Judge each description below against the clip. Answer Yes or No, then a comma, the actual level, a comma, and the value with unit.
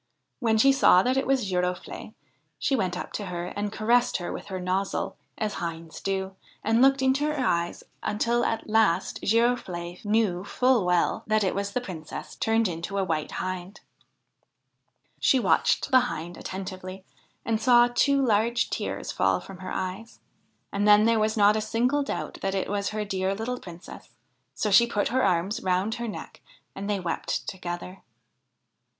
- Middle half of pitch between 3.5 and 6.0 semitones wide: Yes, average, 4.1 semitones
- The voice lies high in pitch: Yes, high, 205 Hz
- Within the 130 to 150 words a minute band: No, average, 175 wpm